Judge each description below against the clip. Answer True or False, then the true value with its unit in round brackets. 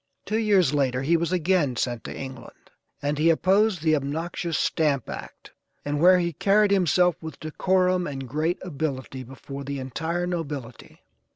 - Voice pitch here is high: False (160 Hz)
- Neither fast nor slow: True (160 wpm)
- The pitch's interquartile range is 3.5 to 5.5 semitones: True (4.6 semitones)